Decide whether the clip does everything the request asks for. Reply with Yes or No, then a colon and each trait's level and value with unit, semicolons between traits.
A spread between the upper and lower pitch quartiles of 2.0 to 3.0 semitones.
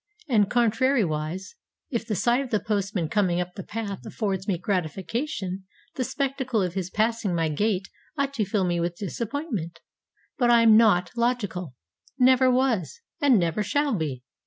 No: average, 5.0 semitones